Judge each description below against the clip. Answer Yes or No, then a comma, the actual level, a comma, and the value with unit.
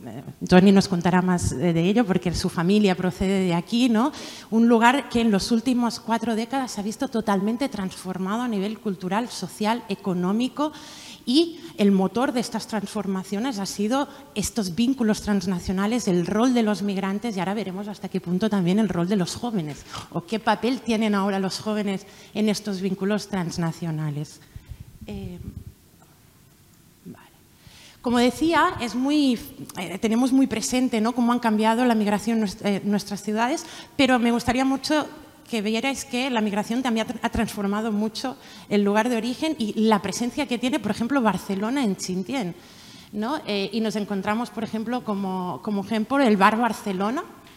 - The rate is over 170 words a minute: No, average, 160 wpm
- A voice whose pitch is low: No, high, 215 Hz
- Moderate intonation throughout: Yes, average, 3.7 semitones